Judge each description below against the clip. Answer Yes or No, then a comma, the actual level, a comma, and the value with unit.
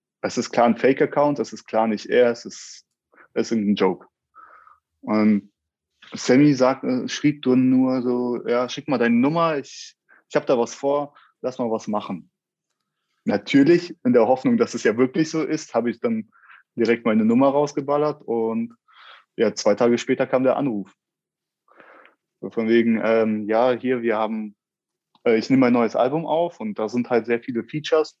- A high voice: No, low, 125 Hz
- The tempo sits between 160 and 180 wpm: Yes, average, 175 wpm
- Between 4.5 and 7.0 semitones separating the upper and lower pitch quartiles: Yes, average, 4.8 semitones